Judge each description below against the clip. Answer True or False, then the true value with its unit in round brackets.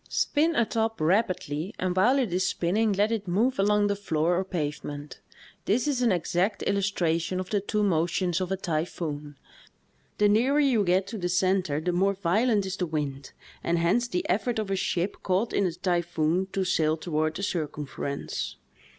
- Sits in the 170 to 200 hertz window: True (185 Hz)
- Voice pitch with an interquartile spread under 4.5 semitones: True (3.6 semitones)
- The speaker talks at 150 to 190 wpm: True (185 wpm)